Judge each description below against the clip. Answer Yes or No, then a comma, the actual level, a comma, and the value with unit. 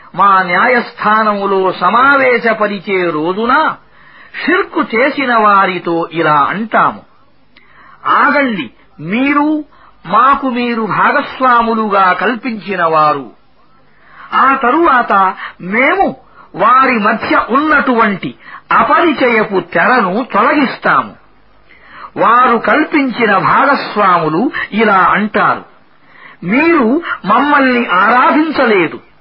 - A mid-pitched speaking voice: No, high, 235 Hz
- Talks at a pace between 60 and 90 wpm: Yes, slow, 65 wpm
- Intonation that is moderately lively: No, wide, 5.9 semitones